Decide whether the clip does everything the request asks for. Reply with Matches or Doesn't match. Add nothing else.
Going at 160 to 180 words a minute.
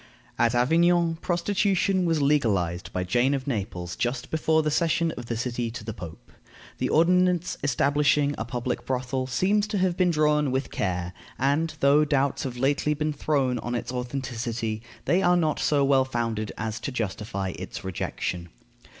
Matches